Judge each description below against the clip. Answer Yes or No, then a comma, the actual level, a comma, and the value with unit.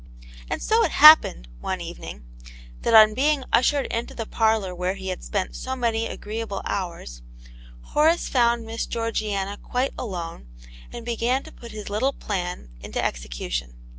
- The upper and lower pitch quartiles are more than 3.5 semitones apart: Yes, average, 4.4 semitones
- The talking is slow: No, average, 160 wpm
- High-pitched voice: Yes, high, 220 Hz